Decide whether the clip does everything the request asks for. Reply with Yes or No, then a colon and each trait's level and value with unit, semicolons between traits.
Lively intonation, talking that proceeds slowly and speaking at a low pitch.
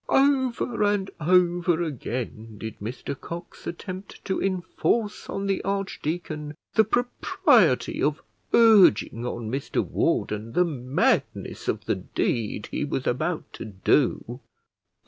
No: wide, 8.1 semitones; slow, 120 wpm; medium, 170 Hz